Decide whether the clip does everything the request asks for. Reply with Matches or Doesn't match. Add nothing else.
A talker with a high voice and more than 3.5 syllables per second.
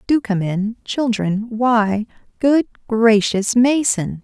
Doesn't match